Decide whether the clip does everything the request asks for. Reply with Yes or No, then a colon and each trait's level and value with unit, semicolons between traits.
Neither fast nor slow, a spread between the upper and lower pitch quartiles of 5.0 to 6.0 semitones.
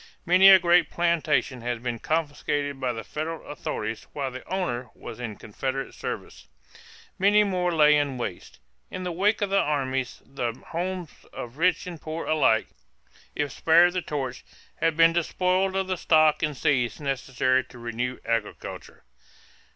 Yes: average, 160 wpm; average, 5.3 semitones